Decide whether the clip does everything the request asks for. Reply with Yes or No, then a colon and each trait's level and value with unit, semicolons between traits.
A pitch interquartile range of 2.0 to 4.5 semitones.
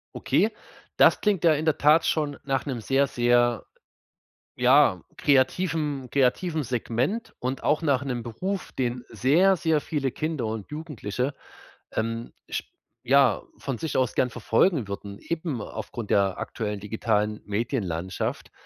No: average, 4.9 semitones